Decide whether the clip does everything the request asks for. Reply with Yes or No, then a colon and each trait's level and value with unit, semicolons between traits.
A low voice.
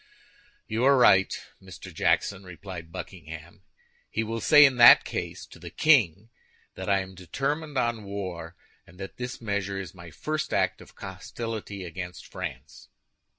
Yes: low, 100 Hz